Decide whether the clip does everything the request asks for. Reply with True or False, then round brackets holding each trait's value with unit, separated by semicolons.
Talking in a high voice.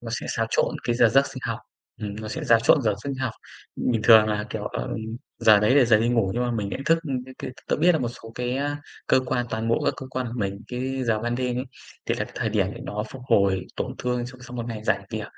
False (120 Hz)